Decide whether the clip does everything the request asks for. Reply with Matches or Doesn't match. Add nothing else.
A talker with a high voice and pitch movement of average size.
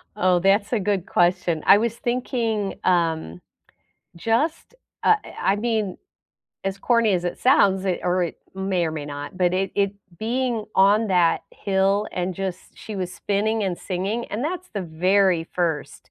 Matches